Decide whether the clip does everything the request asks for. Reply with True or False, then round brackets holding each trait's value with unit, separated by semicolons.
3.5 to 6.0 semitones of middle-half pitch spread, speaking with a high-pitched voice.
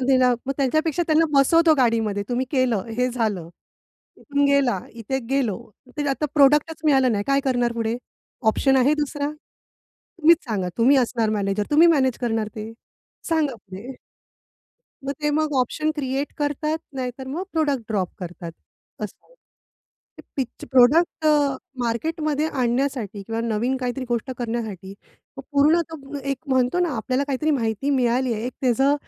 True (4.0 semitones; 260 Hz)